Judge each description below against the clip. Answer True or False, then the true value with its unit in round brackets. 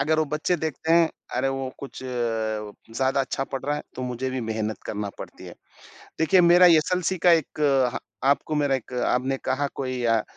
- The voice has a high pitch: False (135 Hz)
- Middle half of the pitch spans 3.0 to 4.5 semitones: True (3.8 semitones)